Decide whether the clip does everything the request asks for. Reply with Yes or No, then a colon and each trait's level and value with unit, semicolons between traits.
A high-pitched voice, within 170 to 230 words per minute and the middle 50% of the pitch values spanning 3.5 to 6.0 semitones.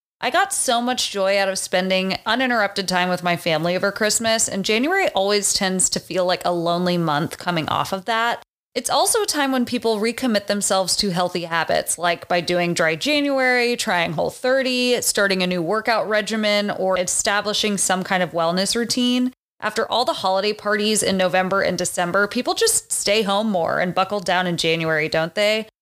Yes: high, 200 Hz; average, 190 wpm; average, 4.0 semitones